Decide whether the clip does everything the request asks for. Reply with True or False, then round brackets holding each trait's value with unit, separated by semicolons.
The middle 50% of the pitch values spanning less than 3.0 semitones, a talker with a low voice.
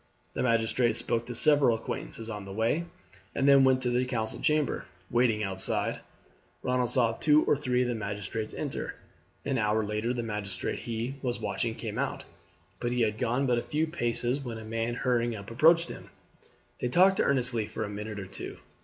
True (2.6 semitones; 120 Hz)